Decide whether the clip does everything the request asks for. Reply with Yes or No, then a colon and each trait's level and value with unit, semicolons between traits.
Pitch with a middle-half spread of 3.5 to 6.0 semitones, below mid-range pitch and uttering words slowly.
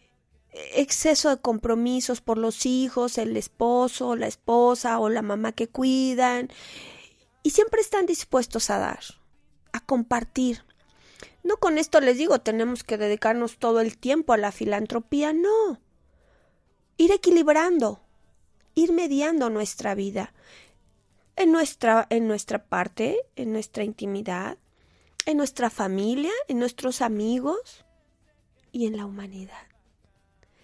No: average, 5.3 semitones; high, 245 Hz; slow, 120 wpm